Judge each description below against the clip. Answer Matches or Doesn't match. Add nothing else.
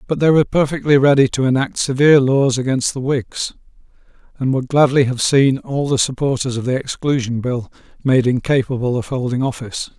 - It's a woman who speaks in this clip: Doesn't match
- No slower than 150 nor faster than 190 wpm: Matches